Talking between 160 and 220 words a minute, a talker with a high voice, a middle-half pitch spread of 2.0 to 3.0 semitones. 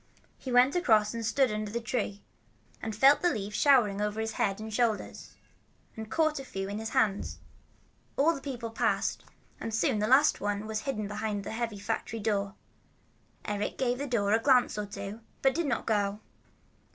No: average, 190 wpm; high, 220 Hz; average, 3.5 semitones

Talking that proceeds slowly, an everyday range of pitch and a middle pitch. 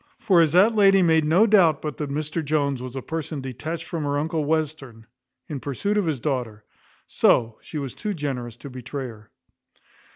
No: average, 190 wpm; average, 3.8 semitones; medium, 150 Hz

